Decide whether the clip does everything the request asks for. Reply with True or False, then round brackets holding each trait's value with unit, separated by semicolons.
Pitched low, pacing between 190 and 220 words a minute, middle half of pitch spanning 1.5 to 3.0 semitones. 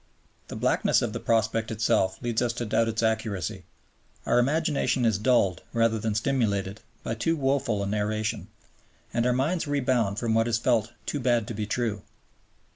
False (115 Hz; 175 wpm; 2.4 semitones)